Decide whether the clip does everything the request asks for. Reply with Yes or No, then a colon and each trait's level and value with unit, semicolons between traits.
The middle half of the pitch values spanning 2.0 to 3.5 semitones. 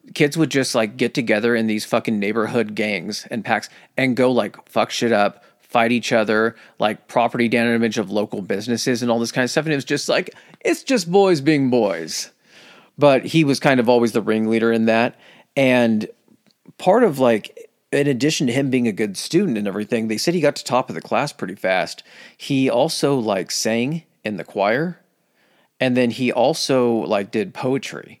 No: average, 4.0 semitones